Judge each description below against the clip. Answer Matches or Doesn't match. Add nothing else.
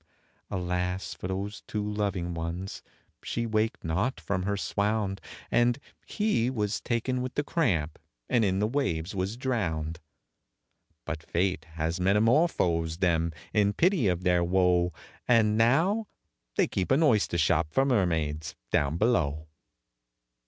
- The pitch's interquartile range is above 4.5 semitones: Matches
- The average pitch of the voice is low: Matches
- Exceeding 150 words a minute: Doesn't match